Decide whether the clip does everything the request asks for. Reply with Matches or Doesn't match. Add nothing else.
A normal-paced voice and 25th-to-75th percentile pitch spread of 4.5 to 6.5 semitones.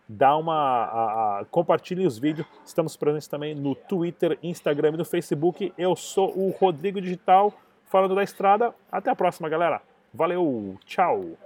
Doesn't match